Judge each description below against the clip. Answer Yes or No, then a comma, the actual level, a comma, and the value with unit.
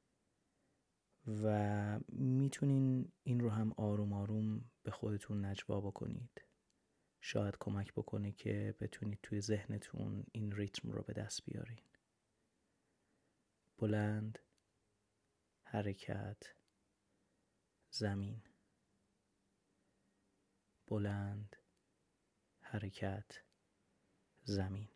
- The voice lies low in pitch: Yes, low, 105 Hz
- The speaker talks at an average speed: No, slow, 70 wpm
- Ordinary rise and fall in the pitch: No, narrow, 1.3 semitones